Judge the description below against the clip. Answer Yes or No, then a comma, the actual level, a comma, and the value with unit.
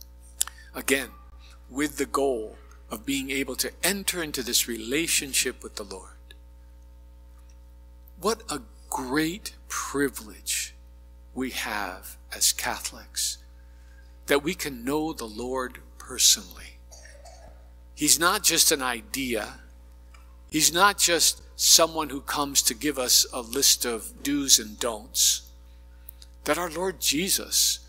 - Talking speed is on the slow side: Yes, slow, 115 wpm